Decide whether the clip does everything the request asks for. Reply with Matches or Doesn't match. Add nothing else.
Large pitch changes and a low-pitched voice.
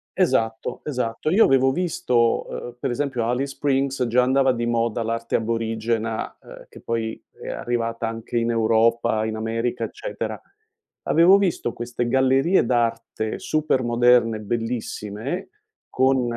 Doesn't match